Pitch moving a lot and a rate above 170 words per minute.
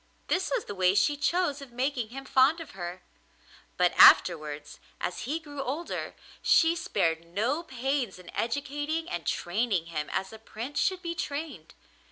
No: wide, 8.1 semitones; average, 165 wpm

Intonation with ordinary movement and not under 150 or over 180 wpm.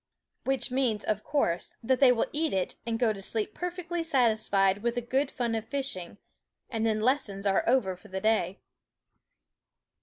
Yes: average, 4.6 semitones; average, 175 wpm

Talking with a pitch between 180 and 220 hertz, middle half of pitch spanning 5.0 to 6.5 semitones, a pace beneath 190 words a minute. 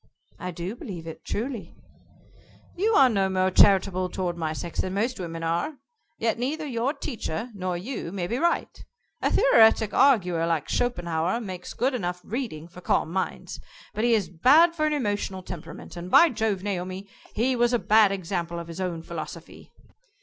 Yes: high, 190 Hz; wide, 5.6 semitones; average, 175 wpm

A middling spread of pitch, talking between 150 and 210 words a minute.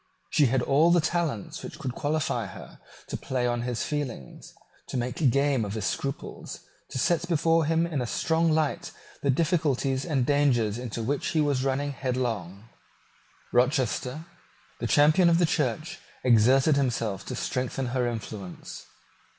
Yes: average, 4.1 semitones; average, 155 wpm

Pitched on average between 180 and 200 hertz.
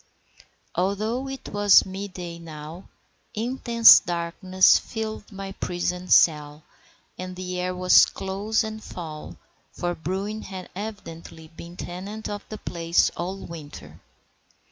Yes: medium, 185 Hz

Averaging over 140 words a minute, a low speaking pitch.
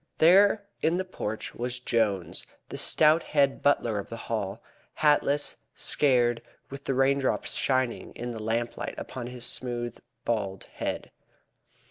No: slow, 135 wpm; low, 125 Hz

